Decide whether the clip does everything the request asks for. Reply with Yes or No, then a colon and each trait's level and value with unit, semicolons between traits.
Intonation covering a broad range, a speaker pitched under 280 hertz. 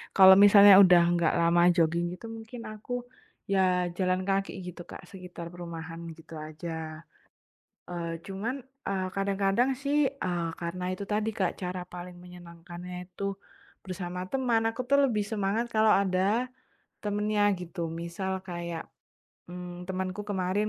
No: average, 3.0 semitones; medium, 185 Hz